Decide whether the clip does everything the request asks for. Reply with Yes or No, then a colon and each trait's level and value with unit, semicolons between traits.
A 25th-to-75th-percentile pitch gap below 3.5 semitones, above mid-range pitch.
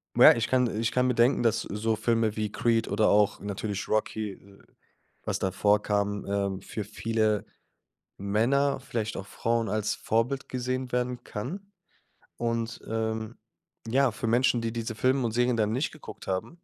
No: average, 2.7 semitones; low, 115 Hz